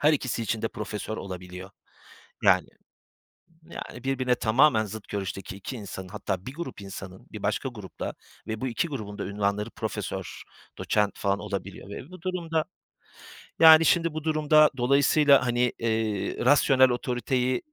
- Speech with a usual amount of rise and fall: No, wide, 5.8 semitones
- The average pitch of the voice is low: Yes, low, 120 Hz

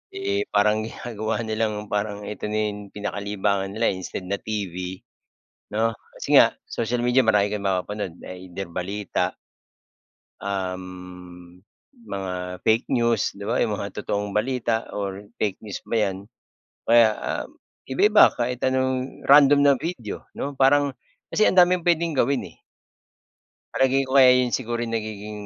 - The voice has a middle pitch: No, low, 110 Hz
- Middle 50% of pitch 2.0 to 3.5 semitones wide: No, average, 4.3 semitones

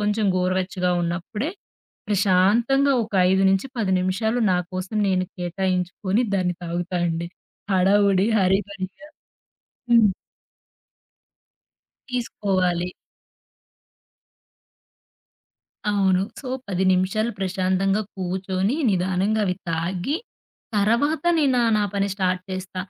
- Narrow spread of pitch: Yes, narrow, 2.3 semitones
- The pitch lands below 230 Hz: Yes, high, 190 Hz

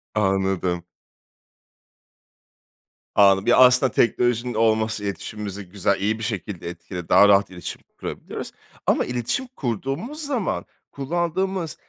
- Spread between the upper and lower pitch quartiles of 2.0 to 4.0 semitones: No, average, 5.2 semitones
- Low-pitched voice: Yes, low, 110 Hz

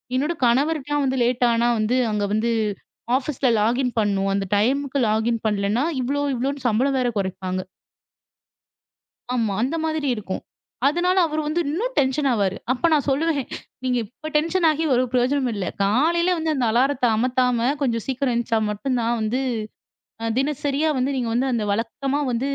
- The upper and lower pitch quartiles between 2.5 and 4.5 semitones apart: Yes, average, 3.9 semitones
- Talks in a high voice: Yes, very high, 255 Hz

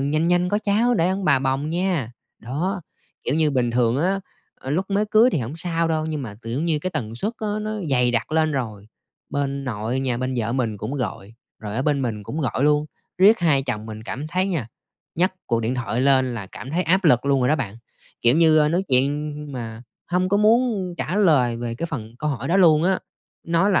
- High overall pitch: No, medium, 145 Hz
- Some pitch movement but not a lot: No, wide, 6.1 semitones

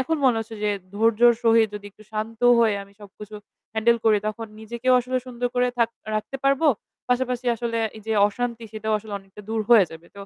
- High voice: Yes, high, 225 Hz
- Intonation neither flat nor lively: No, narrow, 2.1 semitones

